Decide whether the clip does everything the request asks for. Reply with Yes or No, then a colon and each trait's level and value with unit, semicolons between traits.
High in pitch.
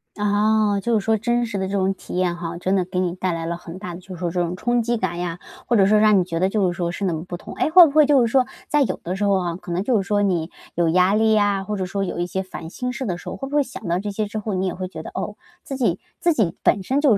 Yes: high, 195 Hz